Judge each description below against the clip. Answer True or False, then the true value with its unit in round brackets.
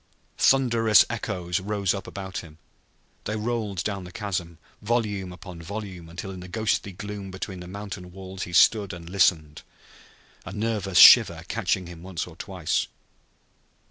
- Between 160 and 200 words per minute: False (150 wpm)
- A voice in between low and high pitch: False (95 Hz)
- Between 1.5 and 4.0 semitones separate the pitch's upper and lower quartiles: True (2.8 semitones)